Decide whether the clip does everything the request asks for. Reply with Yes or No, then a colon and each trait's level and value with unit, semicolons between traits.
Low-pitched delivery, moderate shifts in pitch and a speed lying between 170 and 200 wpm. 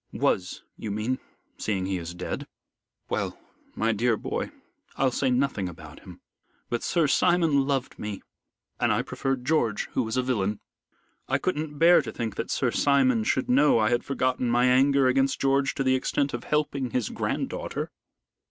Yes: low, 130 Hz; average, 3.8 semitones; average, 175 wpm